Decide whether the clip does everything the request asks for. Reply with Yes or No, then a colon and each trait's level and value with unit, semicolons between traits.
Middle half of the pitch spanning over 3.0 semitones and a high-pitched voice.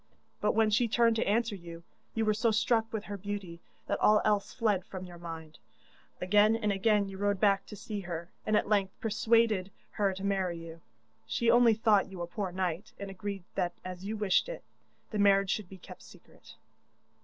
No: narrow, 2.6 semitones; high, 200 Hz